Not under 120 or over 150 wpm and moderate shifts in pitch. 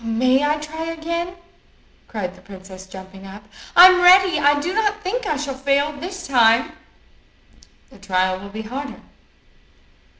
No: average, 145 wpm; wide, 8.8 semitones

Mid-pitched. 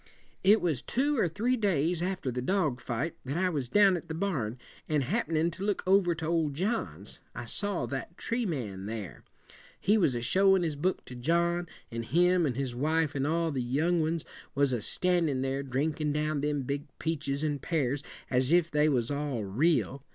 Yes: medium, 155 Hz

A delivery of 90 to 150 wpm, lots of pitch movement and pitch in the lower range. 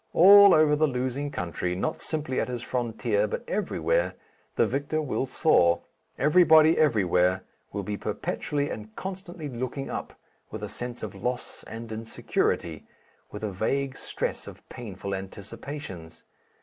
Yes: average, 140 wpm; wide, 6.6 semitones; low, 125 Hz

